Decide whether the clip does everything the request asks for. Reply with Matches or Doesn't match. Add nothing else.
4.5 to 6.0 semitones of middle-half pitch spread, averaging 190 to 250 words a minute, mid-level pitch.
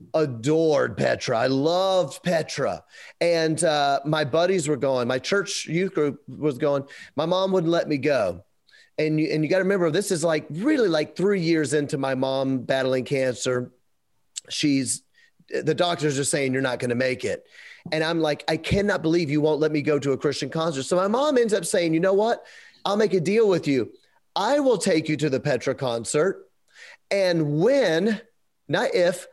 Matches